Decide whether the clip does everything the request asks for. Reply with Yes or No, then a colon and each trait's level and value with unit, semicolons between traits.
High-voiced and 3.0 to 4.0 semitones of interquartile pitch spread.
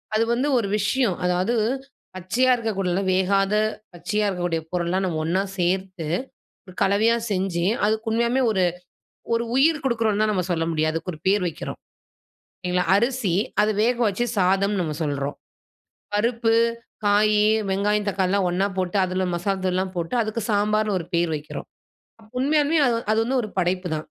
Yes: high, 195 Hz; average, 3.4 semitones